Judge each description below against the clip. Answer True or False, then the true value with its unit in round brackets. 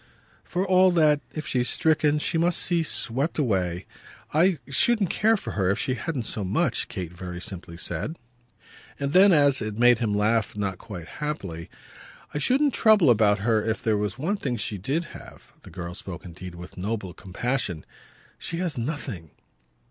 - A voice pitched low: True (120 Hz)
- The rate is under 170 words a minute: False (180 wpm)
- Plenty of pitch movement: True (8.7 semitones)